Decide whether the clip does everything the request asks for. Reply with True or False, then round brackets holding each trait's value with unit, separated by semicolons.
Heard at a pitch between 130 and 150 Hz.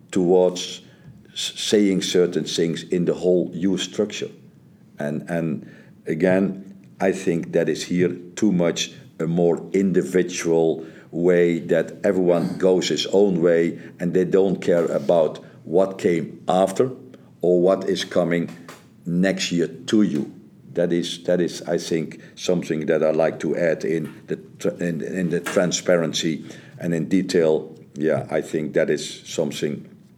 False (90 Hz)